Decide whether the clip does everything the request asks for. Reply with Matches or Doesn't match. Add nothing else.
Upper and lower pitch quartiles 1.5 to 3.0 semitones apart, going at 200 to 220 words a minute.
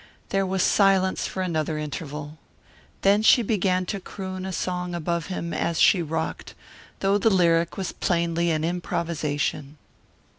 Doesn't match